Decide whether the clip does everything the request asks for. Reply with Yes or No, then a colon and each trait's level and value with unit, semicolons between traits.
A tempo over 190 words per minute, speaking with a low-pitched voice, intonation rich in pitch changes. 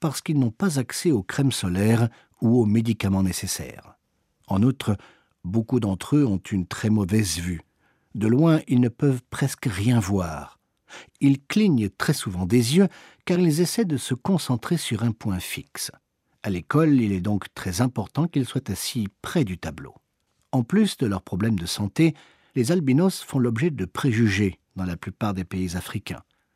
No: average, 175 wpm; low, 120 Hz; wide, 6.3 semitones